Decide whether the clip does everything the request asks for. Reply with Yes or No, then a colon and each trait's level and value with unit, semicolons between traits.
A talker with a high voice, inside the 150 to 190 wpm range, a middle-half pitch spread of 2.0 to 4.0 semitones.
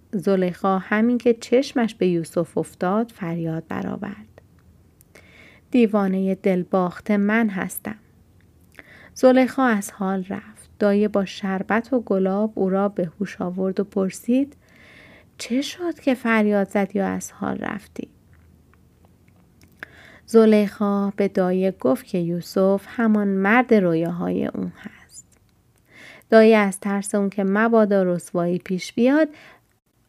No: high, 200 Hz; average, 120 wpm; average, 3.5 semitones